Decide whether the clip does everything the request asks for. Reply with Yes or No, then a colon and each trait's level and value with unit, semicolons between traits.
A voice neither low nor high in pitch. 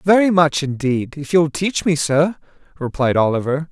Yes: medium, 155 Hz